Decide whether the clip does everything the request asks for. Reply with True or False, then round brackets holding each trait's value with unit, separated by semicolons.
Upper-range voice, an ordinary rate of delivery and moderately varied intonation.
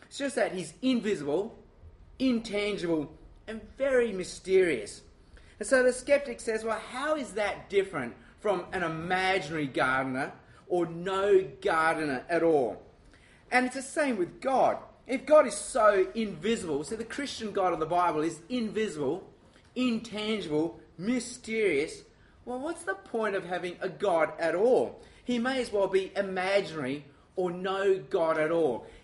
False (205 Hz; 145 wpm; 6.2 semitones)